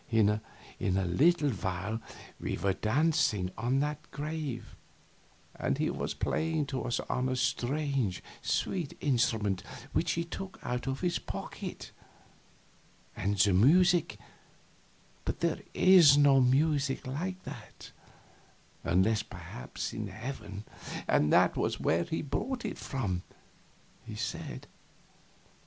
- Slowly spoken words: Yes, slow, 120 wpm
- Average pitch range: No, wide, 6.6 semitones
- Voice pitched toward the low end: Yes, low, 130 Hz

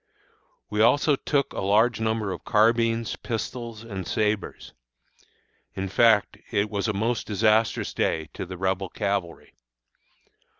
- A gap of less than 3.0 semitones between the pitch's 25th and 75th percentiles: Yes, narrow, 2.6 semitones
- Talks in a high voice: No, low, 110 Hz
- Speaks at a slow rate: Yes, slow, 130 wpm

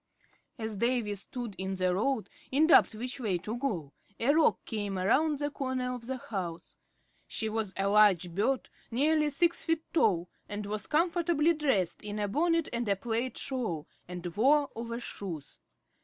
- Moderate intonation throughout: No, wide, 5.8 semitones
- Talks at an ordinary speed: Yes, average, 165 wpm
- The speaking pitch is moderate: No, high, 230 Hz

